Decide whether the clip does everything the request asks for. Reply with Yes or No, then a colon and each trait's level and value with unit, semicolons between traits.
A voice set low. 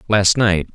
Yes: low, 100 Hz